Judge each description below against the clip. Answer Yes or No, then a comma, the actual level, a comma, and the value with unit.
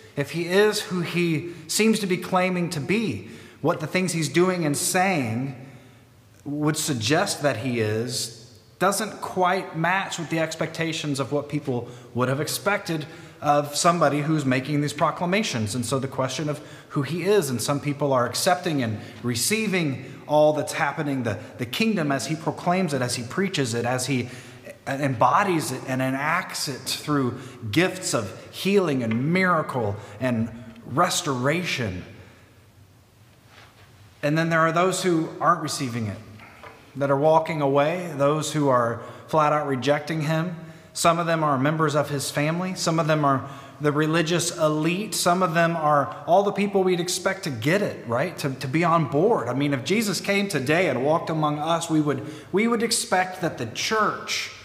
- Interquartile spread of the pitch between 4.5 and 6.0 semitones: Yes, average, 5.0 semitones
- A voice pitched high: No, medium, 150 Hz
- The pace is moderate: Yes, average, 170 wpm